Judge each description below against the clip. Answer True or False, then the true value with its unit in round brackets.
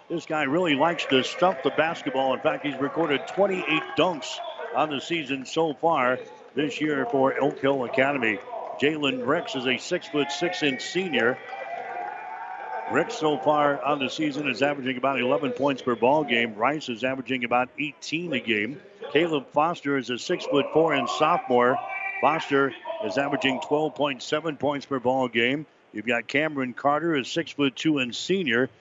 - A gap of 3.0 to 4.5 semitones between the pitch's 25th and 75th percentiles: True (3.3 semitones)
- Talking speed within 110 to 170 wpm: True (150 wpm)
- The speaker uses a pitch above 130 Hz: True (140 Hz)